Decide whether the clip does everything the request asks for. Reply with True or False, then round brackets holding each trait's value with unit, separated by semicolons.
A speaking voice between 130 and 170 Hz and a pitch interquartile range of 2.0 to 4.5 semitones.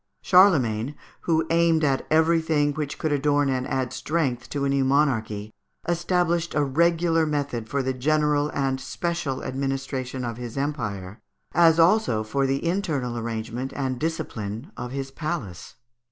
True (140 Hz; 4.2 semitones)